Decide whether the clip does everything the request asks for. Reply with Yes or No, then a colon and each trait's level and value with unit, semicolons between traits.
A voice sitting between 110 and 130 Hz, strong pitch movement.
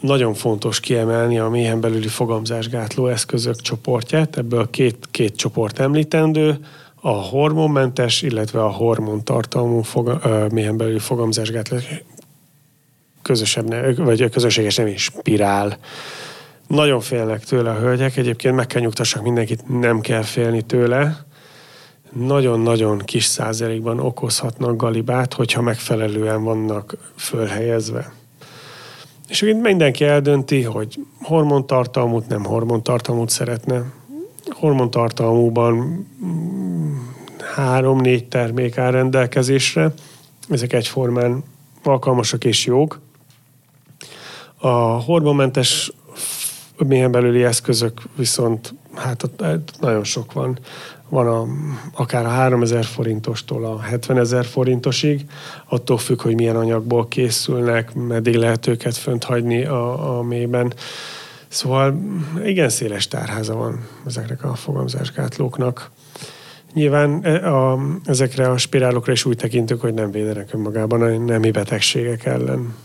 No: low, 125 Hz; average, 3.3 semitones